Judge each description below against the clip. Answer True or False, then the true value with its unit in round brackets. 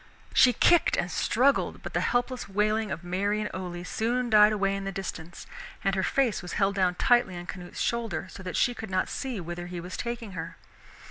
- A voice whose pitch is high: True (195 Hz)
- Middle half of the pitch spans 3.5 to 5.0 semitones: True (4.6 semitones)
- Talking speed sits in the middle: False (210 wpm)